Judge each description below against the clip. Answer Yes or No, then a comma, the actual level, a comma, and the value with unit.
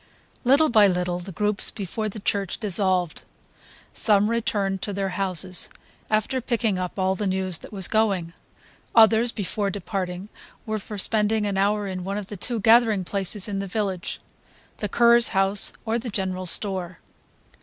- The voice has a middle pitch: No, high, 200 Hz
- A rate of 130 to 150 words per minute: No, average, 165 wpm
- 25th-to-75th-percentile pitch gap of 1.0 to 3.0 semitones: Yes, narrow, 2.5 semitones